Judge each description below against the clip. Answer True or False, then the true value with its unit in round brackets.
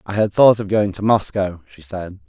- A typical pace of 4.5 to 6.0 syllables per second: True (5.0 syllables/s)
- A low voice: True (100 Hz)